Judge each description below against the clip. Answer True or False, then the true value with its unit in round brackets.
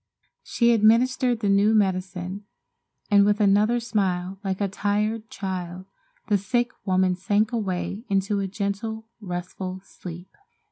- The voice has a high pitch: True (200 Hz)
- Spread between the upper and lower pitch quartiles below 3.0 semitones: True (2.6 semitones)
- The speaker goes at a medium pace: False (130 wpm)